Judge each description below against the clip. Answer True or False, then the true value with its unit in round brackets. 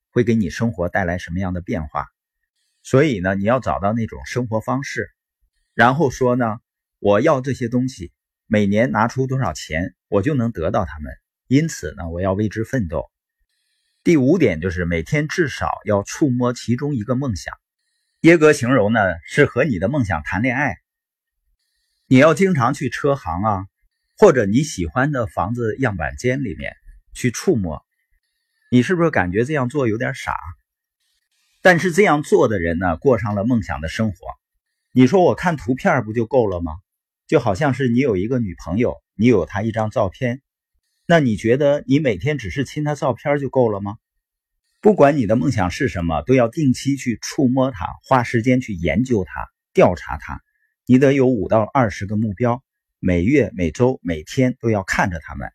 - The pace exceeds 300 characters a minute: False (255 characters per minute)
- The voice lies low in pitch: True (125 Hz)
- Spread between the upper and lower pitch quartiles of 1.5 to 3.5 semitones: False (5.6 semitones)